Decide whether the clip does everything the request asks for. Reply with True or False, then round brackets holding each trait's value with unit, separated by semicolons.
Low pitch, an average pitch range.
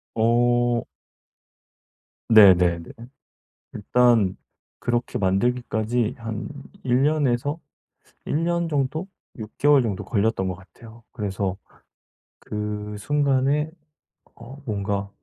True (120 Hz; 4.1 semitones)